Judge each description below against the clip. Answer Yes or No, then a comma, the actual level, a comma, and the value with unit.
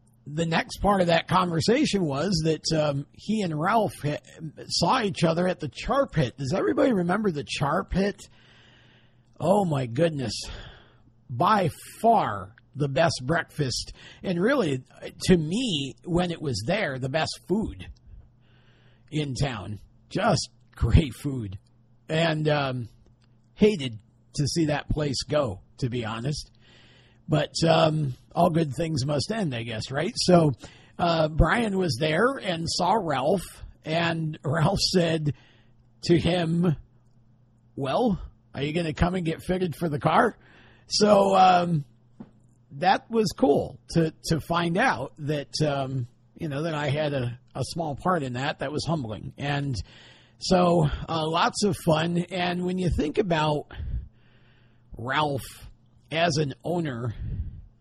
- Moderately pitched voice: Yes, medium, 150 Hz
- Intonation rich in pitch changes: Yes, wide, 6.0 semitones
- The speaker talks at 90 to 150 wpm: Yes, average, 140 wpm